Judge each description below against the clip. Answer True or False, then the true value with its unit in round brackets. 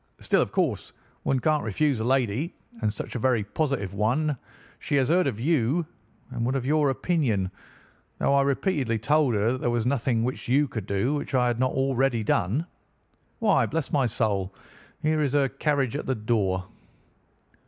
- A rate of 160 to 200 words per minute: True (185 wpm)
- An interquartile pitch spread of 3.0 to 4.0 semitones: False (4.5 semitones)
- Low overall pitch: True (130 Hz)